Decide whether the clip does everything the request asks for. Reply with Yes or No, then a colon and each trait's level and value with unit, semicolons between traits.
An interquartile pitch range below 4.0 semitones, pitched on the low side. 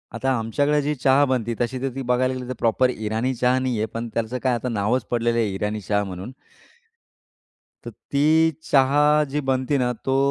Yes: average, 2.7 semitones; low, 125 Hz